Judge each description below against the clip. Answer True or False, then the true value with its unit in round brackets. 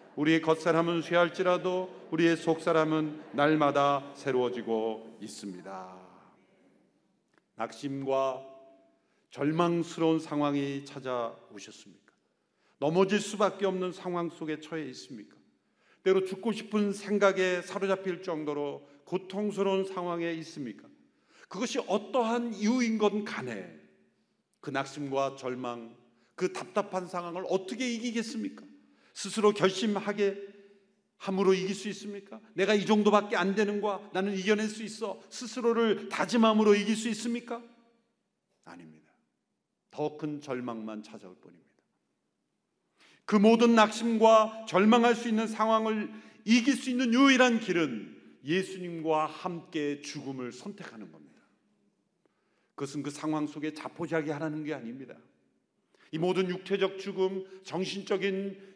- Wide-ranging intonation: True (6.0 semitones)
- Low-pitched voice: False (185 Hz)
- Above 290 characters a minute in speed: False (275 characters per minute)